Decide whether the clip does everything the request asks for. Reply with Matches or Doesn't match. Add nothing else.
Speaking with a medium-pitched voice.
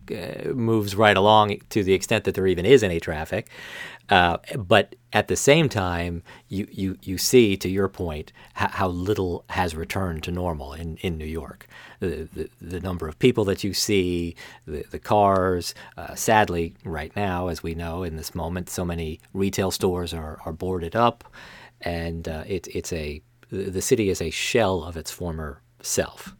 Doesn't match